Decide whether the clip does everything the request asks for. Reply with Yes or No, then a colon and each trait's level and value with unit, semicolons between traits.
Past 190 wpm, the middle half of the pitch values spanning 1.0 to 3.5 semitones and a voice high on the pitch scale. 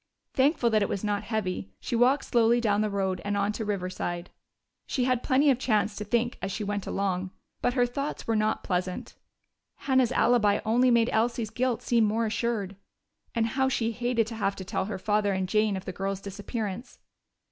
Yes: average, 200 wpm; average, 3.2 semitones; high, 215 Hz